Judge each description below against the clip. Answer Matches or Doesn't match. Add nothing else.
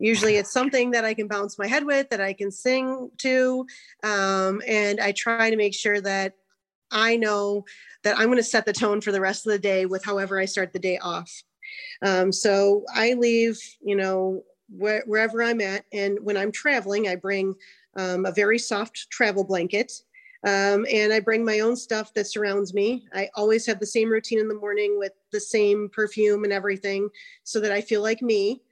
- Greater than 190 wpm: Matches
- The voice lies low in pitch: Doesn't match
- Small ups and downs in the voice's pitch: Matches